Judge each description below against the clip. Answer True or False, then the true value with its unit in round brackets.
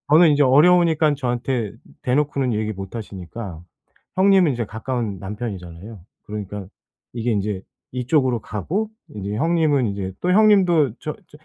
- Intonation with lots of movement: True (6.8 semitones)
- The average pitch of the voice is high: False (120 Hz)